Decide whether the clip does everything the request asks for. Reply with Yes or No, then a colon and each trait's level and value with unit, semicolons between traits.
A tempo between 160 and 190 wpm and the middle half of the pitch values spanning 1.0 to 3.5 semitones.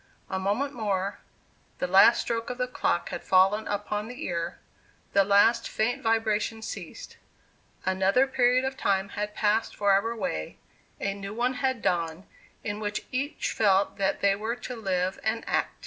Yes: average, 165 wpm; average, 3.2 semitones